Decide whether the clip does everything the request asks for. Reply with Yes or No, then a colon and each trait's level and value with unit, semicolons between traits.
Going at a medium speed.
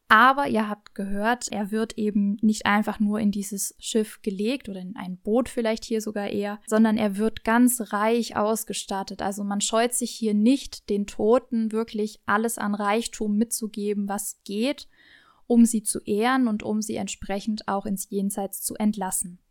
Yes: average, 170 wpm